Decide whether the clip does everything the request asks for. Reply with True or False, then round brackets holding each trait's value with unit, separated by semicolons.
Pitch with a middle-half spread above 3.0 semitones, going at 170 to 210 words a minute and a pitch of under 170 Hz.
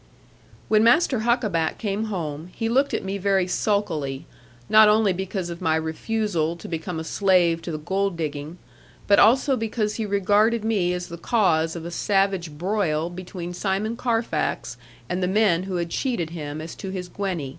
False (4.1 semitones; 175 wpm; 190 Hz)